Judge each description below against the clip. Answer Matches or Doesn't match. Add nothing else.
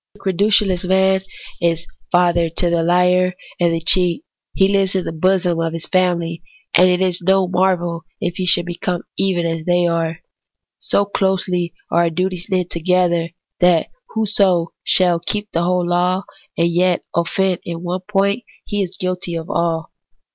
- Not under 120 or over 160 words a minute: Doesn't match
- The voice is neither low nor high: Matches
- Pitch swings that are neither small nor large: Doesn't match